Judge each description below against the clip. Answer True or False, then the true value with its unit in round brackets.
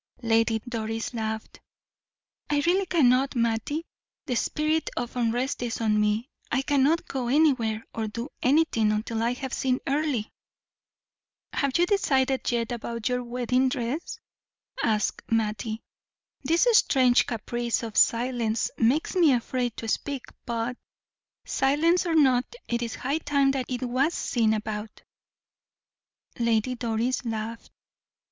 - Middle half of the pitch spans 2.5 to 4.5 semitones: True (3.3 semitones)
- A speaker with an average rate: False (130 wpm)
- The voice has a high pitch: True (245 Hz)